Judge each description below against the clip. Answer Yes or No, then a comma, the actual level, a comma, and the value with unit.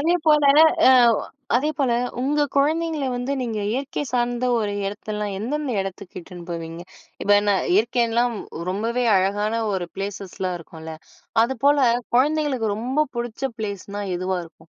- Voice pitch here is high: Yes, high, 225 Hz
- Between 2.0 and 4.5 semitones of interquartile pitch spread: No, average, 5.3 semitones